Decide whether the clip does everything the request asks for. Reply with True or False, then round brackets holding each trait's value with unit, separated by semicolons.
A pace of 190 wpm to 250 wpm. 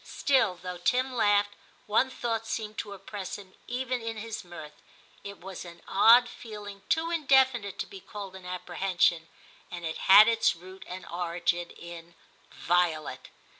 False (155 wpm)